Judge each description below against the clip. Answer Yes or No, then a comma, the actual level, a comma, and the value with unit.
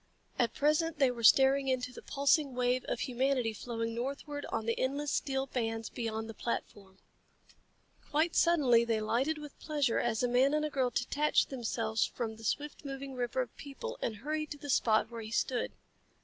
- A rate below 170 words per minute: No, average, 185 wpm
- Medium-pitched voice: No, very high, 255 Hz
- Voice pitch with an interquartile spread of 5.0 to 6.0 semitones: No, average, 3.8 semitones